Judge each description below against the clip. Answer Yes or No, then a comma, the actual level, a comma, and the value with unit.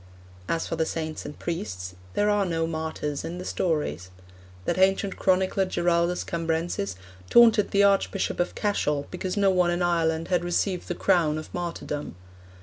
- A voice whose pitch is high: No, medium, 175 Hz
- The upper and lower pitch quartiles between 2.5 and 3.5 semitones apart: Yes, average, 2.8 semitones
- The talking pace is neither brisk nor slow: Yes, average, 160 wpm